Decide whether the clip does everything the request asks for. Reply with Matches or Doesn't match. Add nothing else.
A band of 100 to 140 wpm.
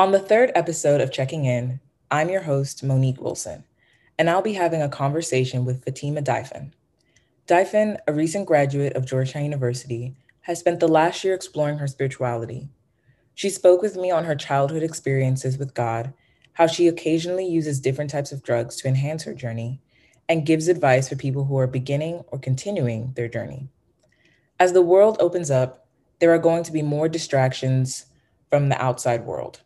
Doesn't match